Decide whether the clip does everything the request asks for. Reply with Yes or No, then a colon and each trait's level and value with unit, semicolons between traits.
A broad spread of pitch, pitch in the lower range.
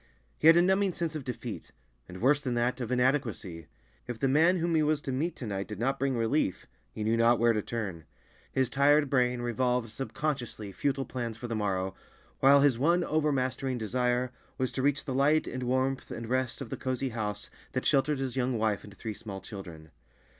No: average, 3.6 semitones; low, 125 Hz